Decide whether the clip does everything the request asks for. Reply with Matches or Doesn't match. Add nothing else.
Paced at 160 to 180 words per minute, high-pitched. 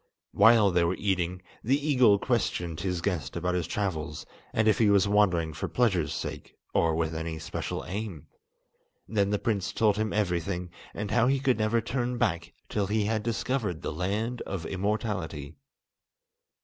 Doesn't match